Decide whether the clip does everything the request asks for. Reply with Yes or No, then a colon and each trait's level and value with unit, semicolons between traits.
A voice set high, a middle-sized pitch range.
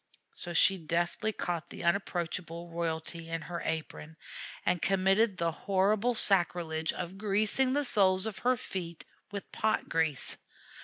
No: medium, 175 Hz; average, 3.2 semitones